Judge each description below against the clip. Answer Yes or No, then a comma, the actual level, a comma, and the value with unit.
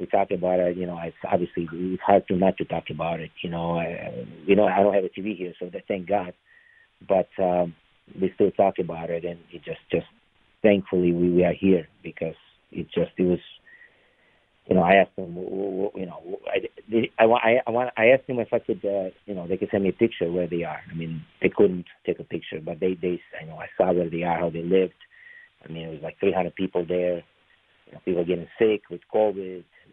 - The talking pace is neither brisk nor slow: No, fast, 235 wpm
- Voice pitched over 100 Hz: No, very low, 90 Hz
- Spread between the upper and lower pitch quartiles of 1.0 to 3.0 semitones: Yes, narrow, 2.5 semitones